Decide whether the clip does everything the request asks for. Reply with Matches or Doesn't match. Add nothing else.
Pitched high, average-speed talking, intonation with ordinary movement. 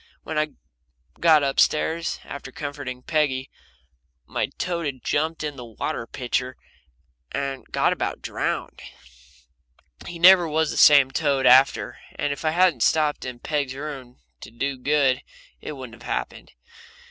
Doesn't match